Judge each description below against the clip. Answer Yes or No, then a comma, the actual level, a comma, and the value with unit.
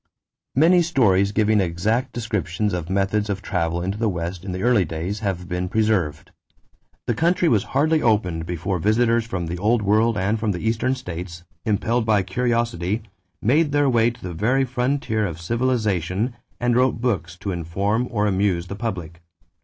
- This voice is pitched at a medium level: No, low, 105 Hz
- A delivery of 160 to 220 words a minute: Yes, average, 175 wpm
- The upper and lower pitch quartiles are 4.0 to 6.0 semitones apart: Yes, average, 4.8 semitones